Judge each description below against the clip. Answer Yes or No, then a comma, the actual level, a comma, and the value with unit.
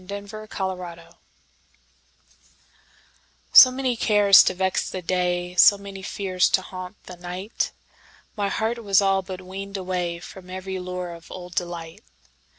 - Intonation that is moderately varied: No, narrow, 1.9 semitones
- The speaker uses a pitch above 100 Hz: Yes, medium, 185 Hz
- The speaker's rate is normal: No, slow, 125 wpm